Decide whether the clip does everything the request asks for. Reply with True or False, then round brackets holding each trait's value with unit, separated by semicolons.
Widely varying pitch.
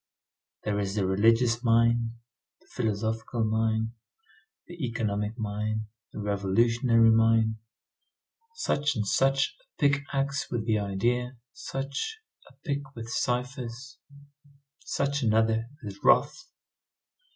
False (3.3 semitones)